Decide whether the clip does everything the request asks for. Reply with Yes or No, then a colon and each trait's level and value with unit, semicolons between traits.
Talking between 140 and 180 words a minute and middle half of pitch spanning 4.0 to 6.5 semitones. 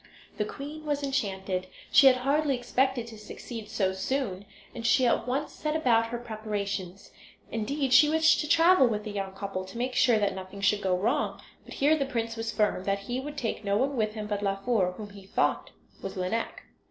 No: fast, 205 wpm; average, 4.9 semitones